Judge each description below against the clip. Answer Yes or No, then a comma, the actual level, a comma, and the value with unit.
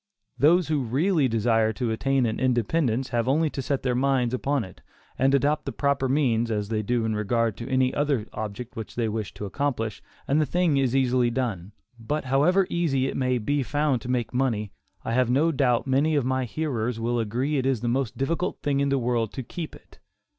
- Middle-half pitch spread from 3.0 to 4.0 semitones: Yes, average, 3.5 semitones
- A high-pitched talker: No, low, 130 Hz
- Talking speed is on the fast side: Yes, fast, 215 wpm